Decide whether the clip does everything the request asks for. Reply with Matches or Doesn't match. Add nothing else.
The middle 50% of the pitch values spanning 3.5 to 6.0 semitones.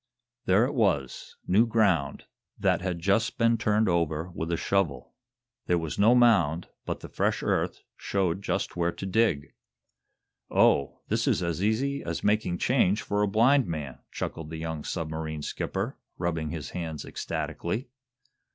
Matches